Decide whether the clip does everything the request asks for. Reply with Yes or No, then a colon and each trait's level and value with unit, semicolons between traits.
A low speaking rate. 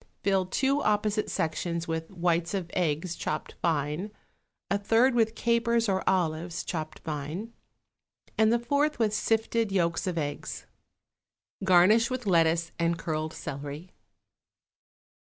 Yes: slow, 125 wpm